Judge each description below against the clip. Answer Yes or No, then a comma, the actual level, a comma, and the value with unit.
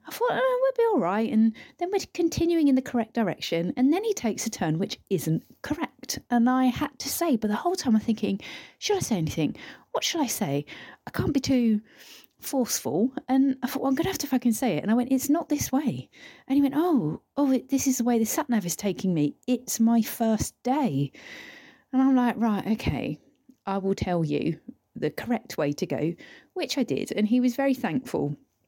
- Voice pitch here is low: No, very high, 250 Hz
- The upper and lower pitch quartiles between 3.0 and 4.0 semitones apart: No, average, 4.6 semitones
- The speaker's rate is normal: No, fast, 225 wpm